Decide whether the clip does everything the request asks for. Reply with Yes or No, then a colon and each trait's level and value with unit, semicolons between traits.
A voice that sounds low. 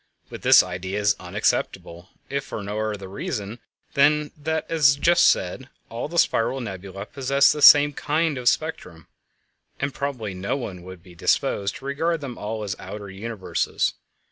Yes: low, 115 Hz